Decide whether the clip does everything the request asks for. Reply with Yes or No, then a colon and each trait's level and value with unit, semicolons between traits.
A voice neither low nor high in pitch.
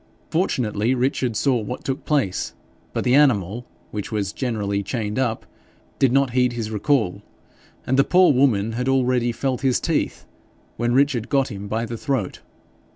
No: low, 125 Hz